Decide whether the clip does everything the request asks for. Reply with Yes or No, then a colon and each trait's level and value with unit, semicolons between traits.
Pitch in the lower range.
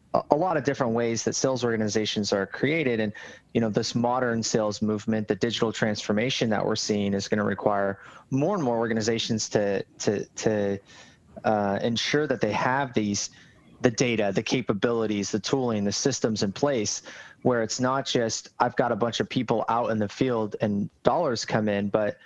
Yes: low, 110 Hz